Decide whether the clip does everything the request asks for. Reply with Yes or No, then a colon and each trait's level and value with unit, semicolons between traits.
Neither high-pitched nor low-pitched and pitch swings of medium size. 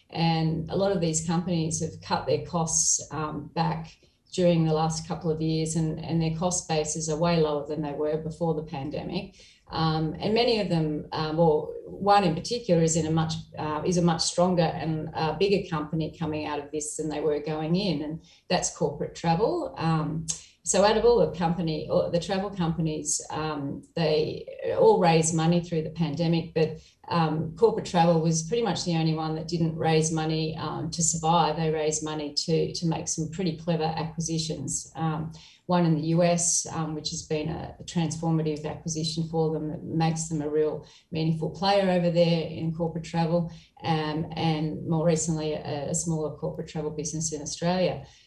No: medium, 160 Hz; narrow, 1.3 semitones